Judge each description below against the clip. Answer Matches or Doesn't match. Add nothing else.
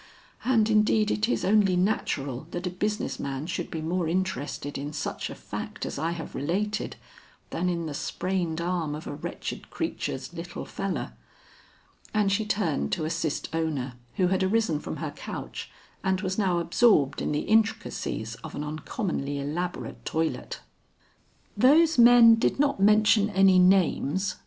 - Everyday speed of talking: Matches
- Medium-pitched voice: Matches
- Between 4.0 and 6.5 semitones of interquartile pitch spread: Matches